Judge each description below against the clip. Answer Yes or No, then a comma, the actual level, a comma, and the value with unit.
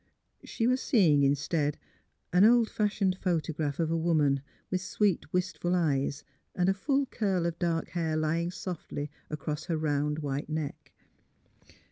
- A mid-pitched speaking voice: Yes, medium, 165 Hz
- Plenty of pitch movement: No, average, 3.8 semitones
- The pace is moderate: Yes, average, 150 wpm